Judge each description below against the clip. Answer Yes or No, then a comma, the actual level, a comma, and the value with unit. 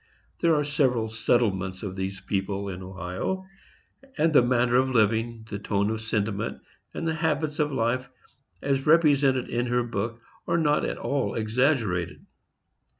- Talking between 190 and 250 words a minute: No, average, 150 wpm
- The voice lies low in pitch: Yes, low, 120 Hz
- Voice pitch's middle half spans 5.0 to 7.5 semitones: Yes, wide, 5.6 semitones